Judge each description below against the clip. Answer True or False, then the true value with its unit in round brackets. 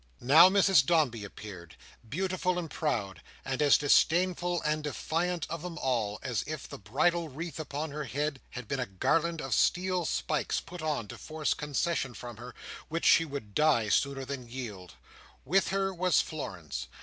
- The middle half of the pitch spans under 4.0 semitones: False (5.5 semitones)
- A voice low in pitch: False (150 Hz)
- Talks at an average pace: True (170 wpm)